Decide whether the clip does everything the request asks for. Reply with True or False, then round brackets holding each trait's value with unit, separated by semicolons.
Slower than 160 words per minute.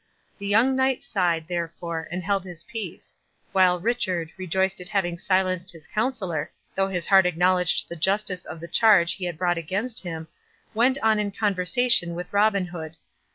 False (170 wpm)